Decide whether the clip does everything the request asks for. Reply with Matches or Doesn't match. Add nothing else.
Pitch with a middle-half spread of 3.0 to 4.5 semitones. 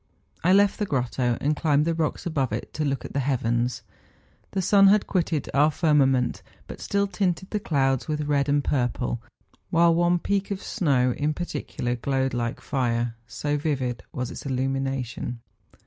Doesn't match